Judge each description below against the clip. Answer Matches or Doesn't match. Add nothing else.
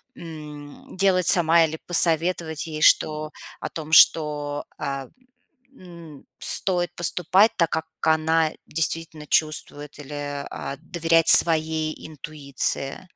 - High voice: Doesn't match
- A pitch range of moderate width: Doesn't match